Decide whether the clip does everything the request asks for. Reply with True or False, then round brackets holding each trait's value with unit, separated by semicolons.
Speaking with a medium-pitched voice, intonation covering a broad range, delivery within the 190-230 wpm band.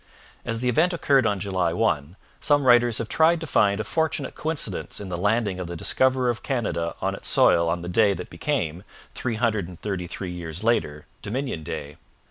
False (105 Hz; 6.2 semitones; 200 wpm)